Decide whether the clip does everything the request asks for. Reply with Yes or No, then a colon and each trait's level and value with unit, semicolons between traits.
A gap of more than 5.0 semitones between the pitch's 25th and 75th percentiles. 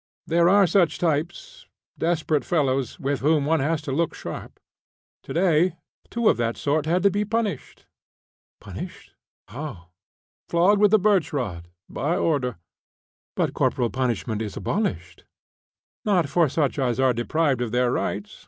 Yes: wide, 5.6 semitones